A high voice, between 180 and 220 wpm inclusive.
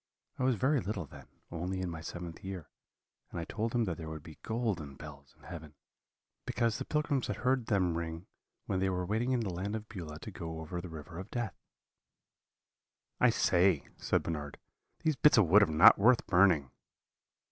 No: very low, 90 Hz; average, 195 wpm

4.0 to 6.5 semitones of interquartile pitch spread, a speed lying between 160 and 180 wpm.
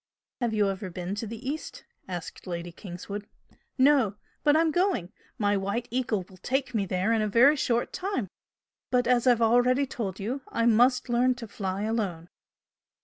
Yes: average, 4.4 semitones; average, 175 wpm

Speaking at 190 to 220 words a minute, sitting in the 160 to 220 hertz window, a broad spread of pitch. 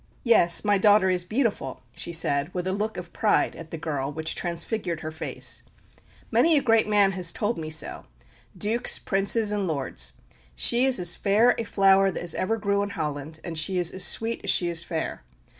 No: average, 195 wpm; high, 190 Hz; average, 4.3 semitones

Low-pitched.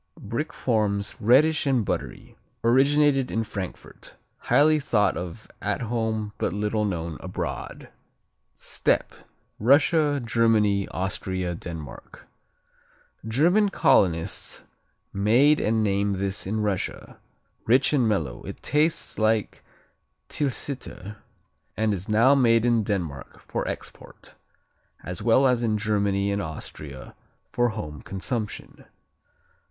Yes: low, 110 Hz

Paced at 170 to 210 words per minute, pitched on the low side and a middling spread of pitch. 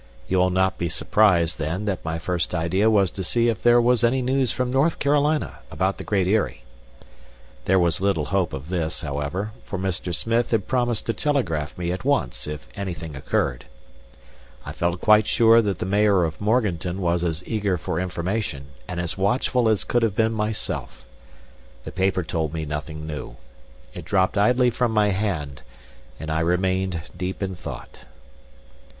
Yes: average, 175 wpm; very low, 95 Hz; average, 4.7 semitones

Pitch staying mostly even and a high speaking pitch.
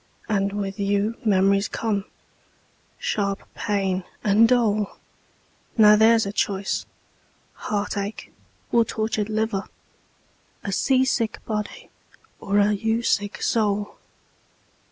Yes: narrow, 1.7 semitones; high, 205 Hz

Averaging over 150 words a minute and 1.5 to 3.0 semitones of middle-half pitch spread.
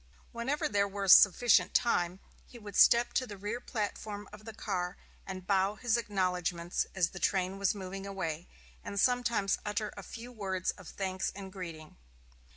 Yes: average, 165 wpm; narrow, 2.4 semitones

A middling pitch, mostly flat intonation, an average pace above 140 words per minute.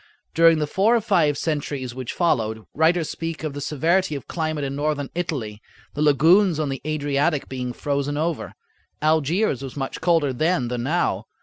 No: medium, 150 Hz; average, 3.3 semitones; average, 175 wpm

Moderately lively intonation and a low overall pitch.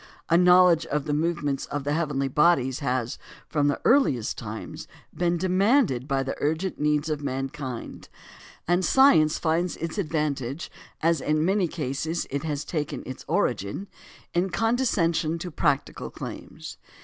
No: average, 3.8 semitones; medium, 155 Hz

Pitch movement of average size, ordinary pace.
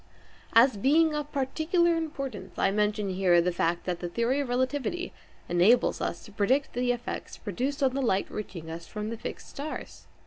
No: wide, 6.2 semitones; average, 180 wpm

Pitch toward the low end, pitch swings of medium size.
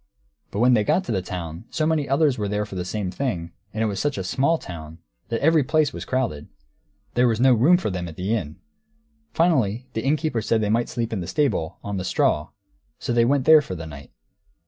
No: low, 115 Hz; wide, 7.1 semitones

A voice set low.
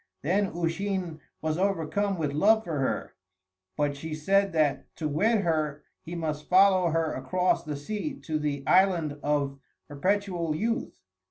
No: medium, 165 Hz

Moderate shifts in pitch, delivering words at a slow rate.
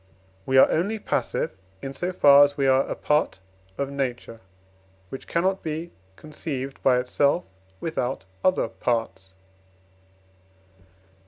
Yes: average, 3.7 semitones; slow, 115 wpm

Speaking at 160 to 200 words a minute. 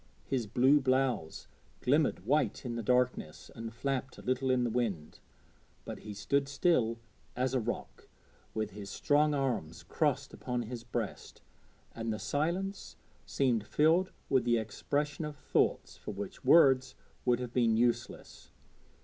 No: average, 150 wpm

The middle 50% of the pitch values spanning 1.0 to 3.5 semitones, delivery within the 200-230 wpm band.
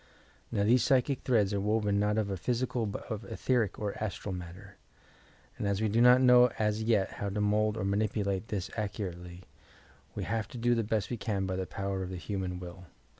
Yes: average, 2.7 semitones; fast, 205 wpm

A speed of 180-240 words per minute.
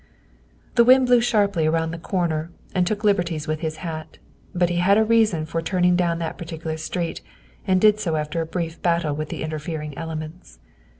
Yes: average, 200 wpm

